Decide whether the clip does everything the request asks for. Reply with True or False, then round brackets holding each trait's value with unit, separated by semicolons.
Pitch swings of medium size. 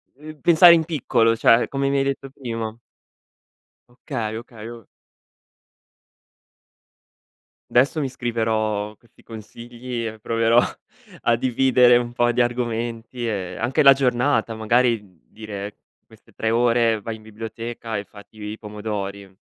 False (2.2 semitones)